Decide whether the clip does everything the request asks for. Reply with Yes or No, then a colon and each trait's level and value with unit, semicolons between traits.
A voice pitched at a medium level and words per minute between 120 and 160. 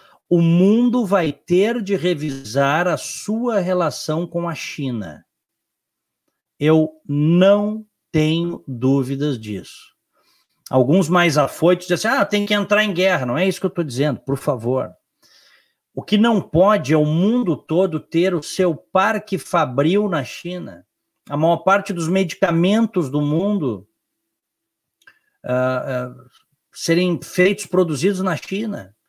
Yes: medium, 175 Hz; average, 135 wpm